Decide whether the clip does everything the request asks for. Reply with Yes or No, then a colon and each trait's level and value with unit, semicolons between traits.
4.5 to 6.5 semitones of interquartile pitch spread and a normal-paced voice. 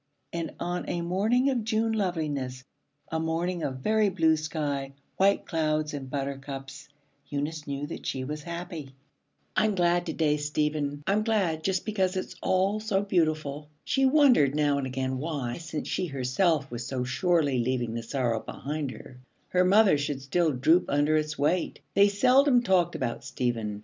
Yes: average, 5.0 semitones; average, 170 wpm